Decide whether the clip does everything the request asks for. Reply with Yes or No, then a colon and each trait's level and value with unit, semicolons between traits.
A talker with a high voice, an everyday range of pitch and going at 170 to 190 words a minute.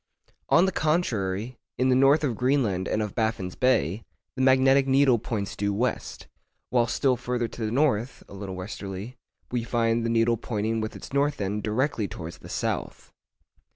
No: low, 115 Hz; average, 3.9 semitones; average, 175 wpm